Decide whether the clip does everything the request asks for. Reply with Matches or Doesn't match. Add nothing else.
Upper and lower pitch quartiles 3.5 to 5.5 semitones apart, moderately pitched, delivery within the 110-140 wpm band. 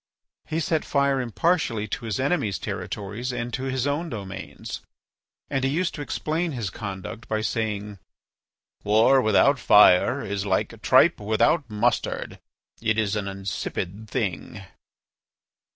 Doesn't match